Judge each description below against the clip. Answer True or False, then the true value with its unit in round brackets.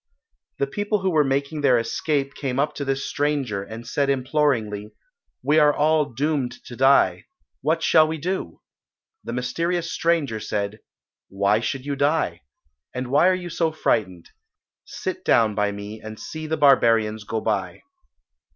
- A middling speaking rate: True (160 wpm)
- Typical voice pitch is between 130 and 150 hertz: True (135 Hz)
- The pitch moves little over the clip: False (5.6 semitones)